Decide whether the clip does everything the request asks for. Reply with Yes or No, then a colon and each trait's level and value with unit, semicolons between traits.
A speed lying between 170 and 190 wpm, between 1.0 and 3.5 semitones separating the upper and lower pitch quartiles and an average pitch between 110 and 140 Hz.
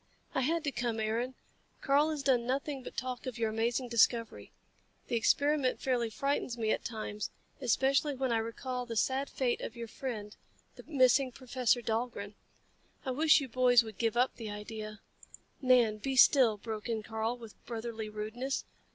No: average, 175 wpm; average, 2.9 semitones; high, 240 Hz